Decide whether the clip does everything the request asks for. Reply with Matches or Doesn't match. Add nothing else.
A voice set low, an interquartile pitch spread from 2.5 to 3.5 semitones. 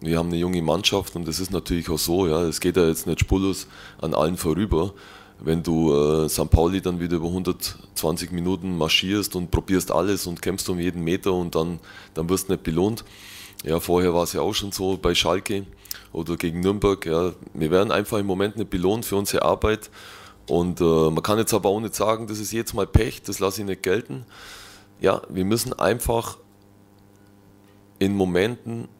Matches